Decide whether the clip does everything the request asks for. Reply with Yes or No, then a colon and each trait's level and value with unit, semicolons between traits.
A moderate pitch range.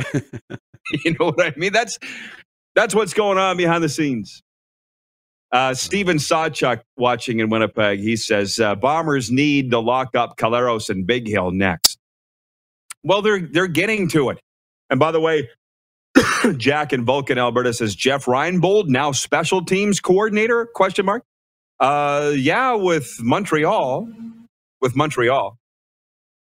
No: wide, 6.9 semitones